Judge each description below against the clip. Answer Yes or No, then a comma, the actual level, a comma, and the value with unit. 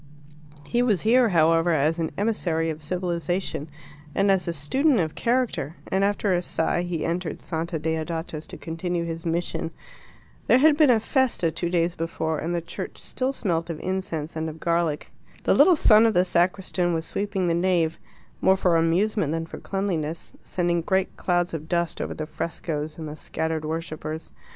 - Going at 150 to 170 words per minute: No, average, 180 wpm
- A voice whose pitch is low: No, medium, 170 Hz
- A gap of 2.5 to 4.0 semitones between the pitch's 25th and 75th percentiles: Yes, average, 2.9 semitones